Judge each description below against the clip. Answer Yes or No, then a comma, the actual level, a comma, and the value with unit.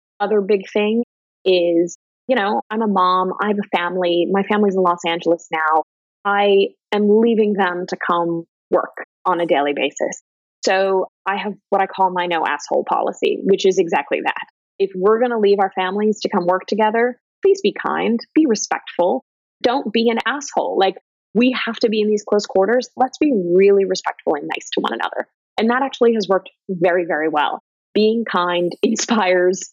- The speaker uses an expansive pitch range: No, average, 3.9 semitones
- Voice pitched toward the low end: No, high, 200 Hz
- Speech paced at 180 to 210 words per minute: Yes, average, 190 wpm